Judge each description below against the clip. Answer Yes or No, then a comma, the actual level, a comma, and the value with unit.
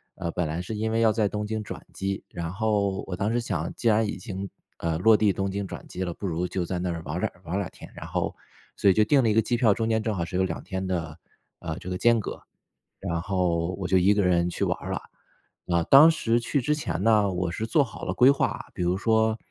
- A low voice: Yes, low, 100 Hz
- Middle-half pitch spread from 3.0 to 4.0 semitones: Yes, average, 3.7 semitones